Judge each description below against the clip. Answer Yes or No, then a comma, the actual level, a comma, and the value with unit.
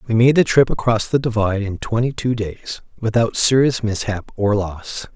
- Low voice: Yes, low, 110 Hz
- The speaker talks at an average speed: Yes, average, 185 wpm